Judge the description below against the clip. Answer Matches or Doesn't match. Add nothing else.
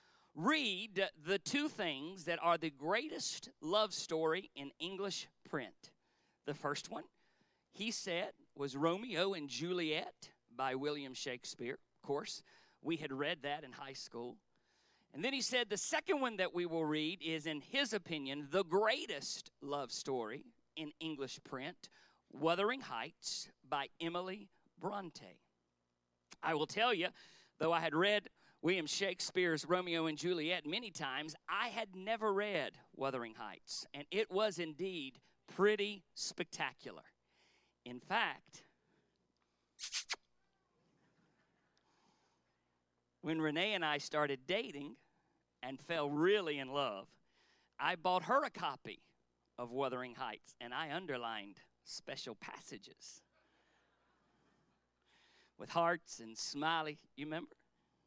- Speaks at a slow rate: Matches